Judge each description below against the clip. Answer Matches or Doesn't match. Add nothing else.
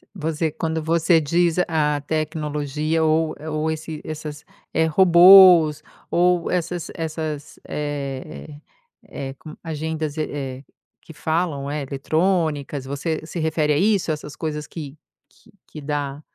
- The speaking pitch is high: Doesn't match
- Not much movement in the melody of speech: Matches